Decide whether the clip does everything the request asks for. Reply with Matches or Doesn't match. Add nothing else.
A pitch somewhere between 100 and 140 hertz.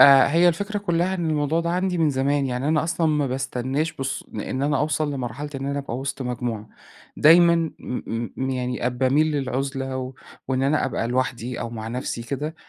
Matches